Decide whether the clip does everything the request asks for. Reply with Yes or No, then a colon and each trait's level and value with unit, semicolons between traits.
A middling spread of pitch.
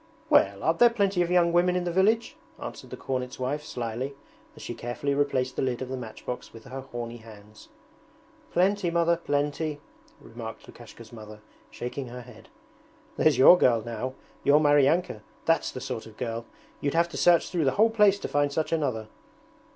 No: wide, 6.1 semitones